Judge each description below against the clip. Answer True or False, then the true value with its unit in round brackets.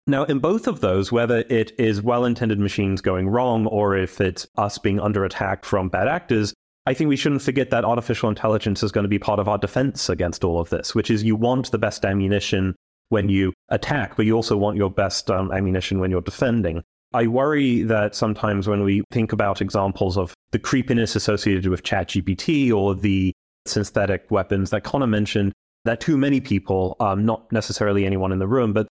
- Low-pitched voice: True (105 Hz)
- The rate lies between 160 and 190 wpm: False (205 wpm)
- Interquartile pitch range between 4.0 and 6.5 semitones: False (3.1 semitones)